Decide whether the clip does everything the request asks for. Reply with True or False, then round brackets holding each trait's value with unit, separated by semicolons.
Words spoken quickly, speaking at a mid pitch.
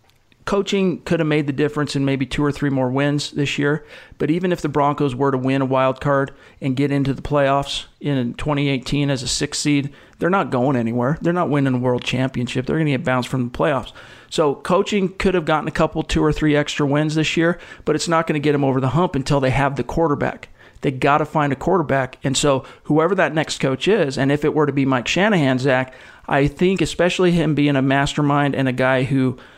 True (235 wpm; 145 Hz)